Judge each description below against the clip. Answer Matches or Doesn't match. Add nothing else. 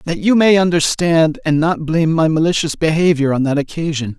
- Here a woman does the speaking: Doesn't match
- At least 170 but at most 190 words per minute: Matches